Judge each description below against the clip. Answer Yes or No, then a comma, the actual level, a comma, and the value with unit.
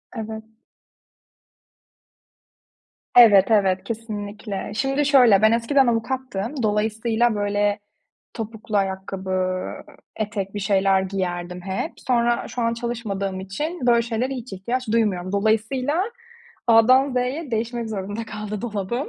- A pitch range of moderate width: Yes, average, 3.4 semitones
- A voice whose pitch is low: No, high, 220 Hz